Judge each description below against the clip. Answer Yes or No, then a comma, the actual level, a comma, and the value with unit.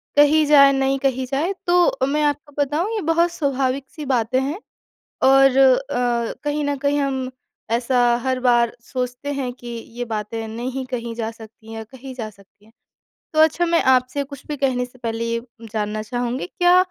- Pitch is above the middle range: Yes, very high, 260 Hz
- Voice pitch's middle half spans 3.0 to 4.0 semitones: Yes, average, 3.3 semitones